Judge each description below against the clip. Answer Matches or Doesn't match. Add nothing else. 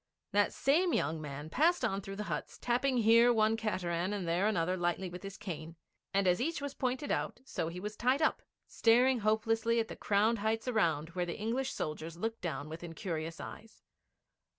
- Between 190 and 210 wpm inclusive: Matches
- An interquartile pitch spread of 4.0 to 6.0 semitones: Matches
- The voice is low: Doesn't match